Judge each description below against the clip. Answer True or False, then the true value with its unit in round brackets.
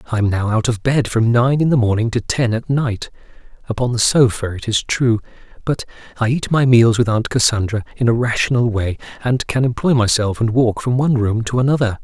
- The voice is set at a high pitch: False (120 Hz)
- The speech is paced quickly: True (220 wpm)